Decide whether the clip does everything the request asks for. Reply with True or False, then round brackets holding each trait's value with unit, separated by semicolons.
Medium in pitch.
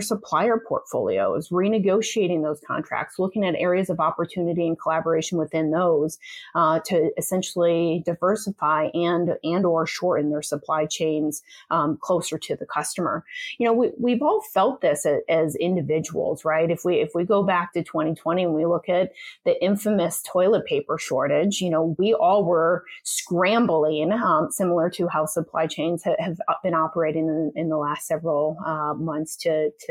True (170 Hz)